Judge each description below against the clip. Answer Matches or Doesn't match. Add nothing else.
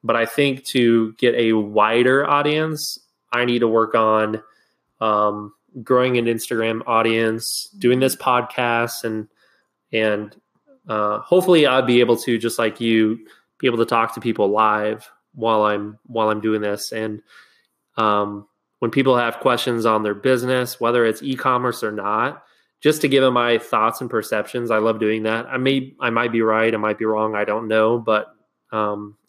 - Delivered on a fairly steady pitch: Matches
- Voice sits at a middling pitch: Doesn't match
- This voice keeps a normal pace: Matches